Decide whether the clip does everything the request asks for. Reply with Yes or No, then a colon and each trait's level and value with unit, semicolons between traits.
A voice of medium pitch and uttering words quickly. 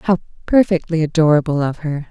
No: medium, 160 Hz; average, 140 wpm